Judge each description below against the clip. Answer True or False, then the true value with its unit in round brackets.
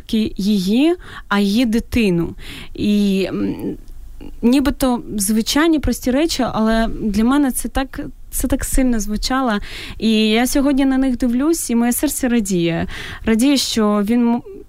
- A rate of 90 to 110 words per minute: False (125 wpm)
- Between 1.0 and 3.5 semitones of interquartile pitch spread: False (4.1 semitones)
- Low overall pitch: False (240 Hz)